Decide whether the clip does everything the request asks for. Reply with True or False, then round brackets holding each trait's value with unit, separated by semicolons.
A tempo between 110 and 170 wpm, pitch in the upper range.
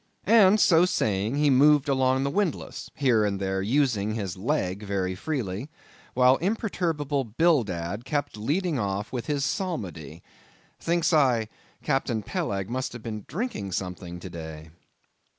False (140 wpm; 125 Hz)